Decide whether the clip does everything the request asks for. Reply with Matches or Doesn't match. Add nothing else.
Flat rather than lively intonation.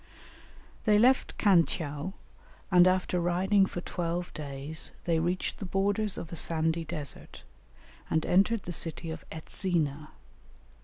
Doesn't match